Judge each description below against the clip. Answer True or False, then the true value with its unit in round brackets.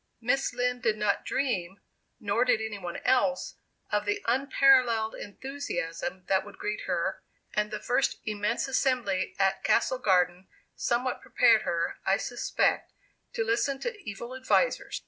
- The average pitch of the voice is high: True (235 Hz)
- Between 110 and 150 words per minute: True (145 wpm)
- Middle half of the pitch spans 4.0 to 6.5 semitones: True (4.5 semitones)